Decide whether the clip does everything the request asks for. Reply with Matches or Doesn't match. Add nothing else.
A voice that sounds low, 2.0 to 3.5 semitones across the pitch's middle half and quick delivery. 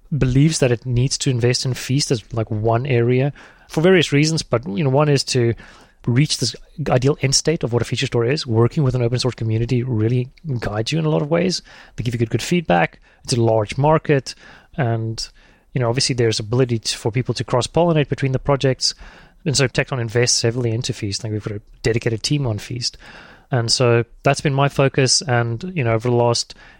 Matches